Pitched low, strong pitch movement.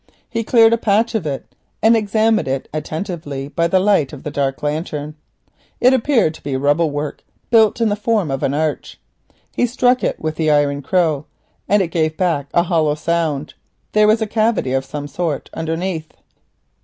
No: medium, 165 Hz; wide, 6.4 semitones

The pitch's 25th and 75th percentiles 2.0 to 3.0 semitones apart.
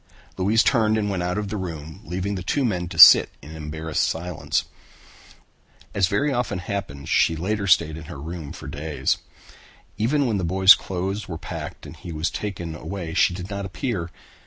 No: average, 3.8 semitones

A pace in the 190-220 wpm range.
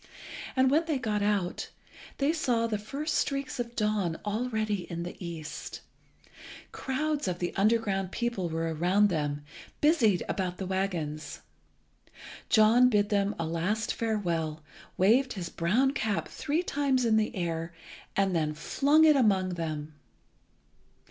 No: average, 140 wpm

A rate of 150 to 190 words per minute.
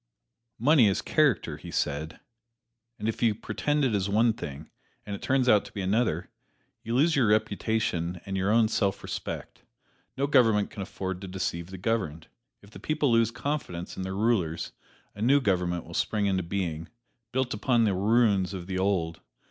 Yes: average, 180 wpm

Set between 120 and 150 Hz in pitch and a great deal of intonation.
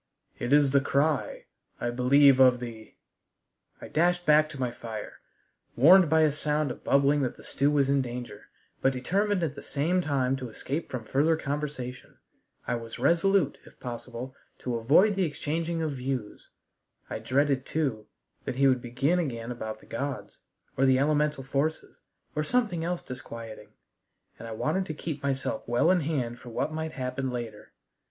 No: medium, 140 Hz; average, 3.7 semitones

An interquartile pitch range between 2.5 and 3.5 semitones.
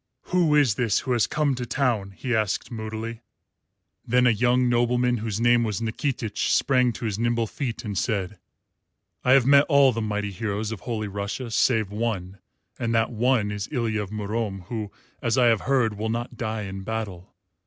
Yes: average, 2.8 semitones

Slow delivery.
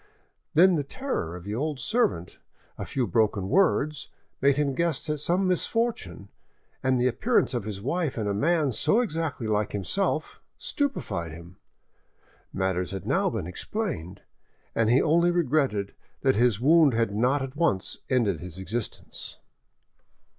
No: average, 155 wpm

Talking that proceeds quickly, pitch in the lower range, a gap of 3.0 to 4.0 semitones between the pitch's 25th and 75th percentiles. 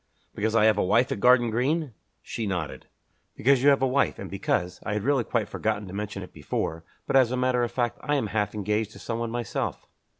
Yes: fast, 230 wpm; low, 115 Hz; average, 3.6 semitones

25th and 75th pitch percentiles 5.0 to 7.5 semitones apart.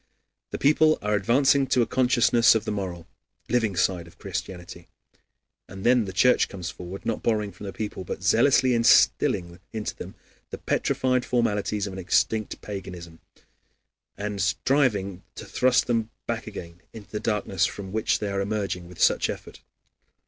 No: average, 3.9 semitones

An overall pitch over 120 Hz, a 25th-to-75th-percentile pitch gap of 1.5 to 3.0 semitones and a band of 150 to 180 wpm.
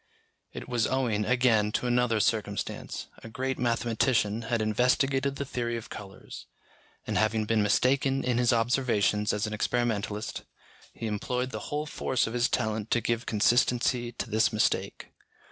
No: low, 115 Hz; narrow, 2.6 semitones; average, 155 wpm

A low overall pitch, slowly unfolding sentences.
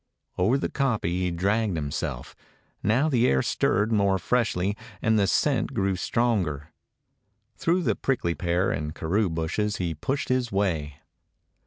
No: very low, 95 Hz; average, 145 wpm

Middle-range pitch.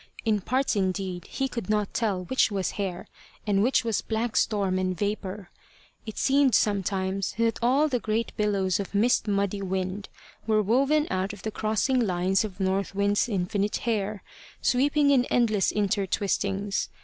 No: high, 205 Hz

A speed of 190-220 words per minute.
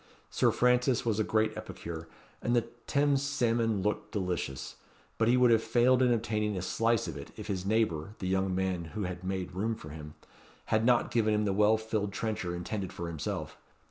Yes: average, 200 wpm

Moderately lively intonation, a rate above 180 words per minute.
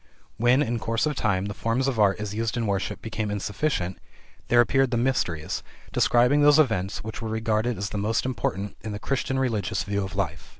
Yes: average, 3.4 semitones; fast, 205 wpm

